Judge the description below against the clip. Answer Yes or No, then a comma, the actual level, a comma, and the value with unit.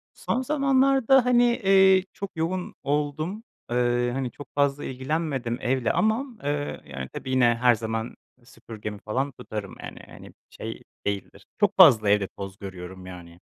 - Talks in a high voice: No, low, 130 Hz